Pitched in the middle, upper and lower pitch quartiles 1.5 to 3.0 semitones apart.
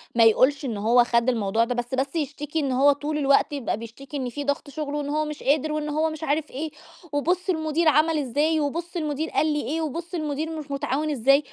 No: very high, 290 Hz; narrow, 2.6 semitones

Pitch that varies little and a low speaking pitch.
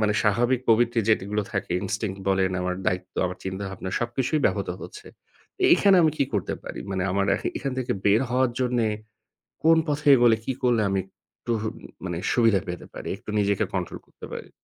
No: average, 4.3 semitones; low, 110 Hz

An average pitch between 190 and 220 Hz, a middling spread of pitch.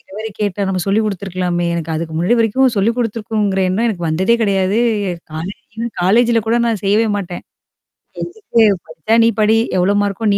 Yes: high, 200 Hz; average, 3.6 semitones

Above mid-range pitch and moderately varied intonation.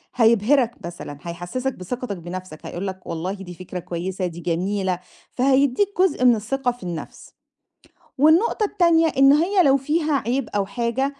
No: high, 235 Hz; wide, 7.0 semitones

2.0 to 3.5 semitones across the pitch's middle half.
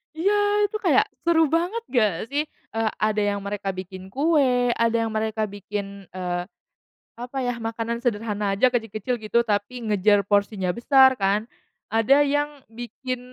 No: average, 3.9 semitones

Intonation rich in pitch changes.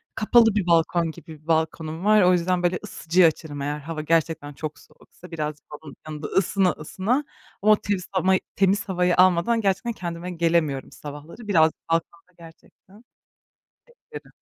No: average, 3.2 semitones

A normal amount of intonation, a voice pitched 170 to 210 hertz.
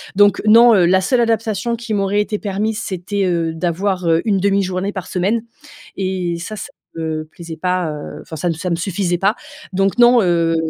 Yes: average, 3.3 semitones; high, 190 Hz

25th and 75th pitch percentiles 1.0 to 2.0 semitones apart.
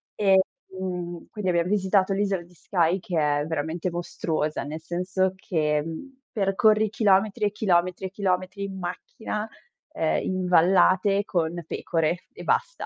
No: narrow, 2.4 semitones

